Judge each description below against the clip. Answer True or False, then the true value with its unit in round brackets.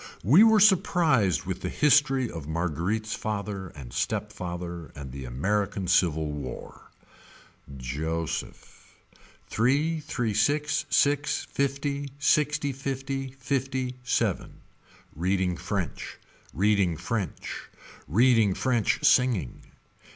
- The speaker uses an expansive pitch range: True (8.1 semitones)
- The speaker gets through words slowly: True (100 wpm)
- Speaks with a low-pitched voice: True (110 Hz)